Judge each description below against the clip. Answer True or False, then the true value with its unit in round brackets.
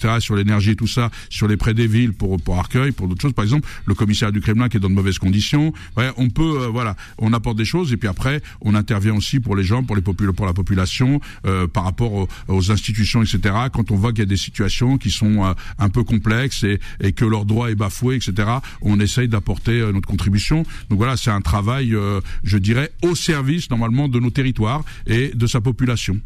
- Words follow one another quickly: True (240 wpm)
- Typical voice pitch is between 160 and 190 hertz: False (110 Hz)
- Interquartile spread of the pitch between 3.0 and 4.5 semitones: True (3.3 semitones)